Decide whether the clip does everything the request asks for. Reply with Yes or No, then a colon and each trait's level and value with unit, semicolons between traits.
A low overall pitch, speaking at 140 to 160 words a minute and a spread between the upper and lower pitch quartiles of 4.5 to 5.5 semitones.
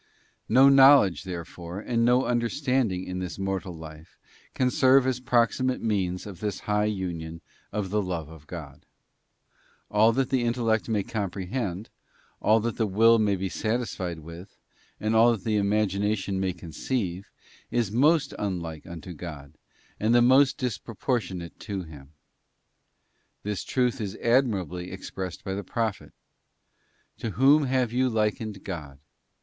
Yes: low, 105 Hz; average, 155 wpm; average, 4.8 semitones